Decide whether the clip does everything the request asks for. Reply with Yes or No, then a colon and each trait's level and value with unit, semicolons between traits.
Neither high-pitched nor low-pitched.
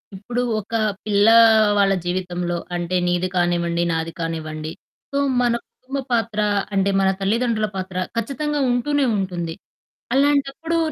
No: high, 195 Hz